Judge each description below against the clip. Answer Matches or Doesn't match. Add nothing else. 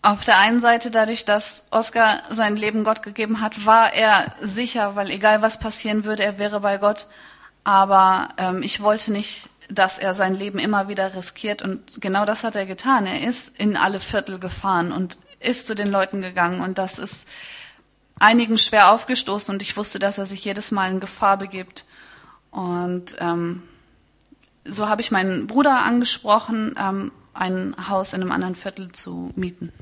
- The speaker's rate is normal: Matches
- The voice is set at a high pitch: Matches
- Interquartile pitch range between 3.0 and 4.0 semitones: Doesn't match